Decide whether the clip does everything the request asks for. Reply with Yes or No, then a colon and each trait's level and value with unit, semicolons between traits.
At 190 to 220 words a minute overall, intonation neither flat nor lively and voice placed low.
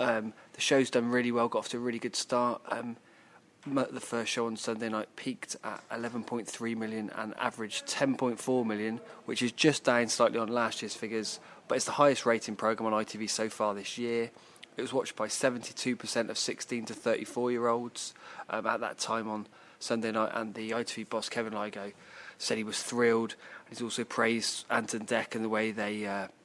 No: average, 195 wpm; narrow, 1.4 semitones; low, 115 Hz